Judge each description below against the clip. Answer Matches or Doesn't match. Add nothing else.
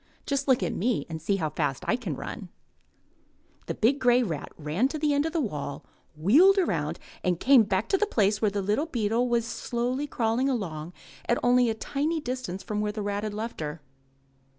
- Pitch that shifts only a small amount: Doesn't match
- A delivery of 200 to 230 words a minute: Matches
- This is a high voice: Matches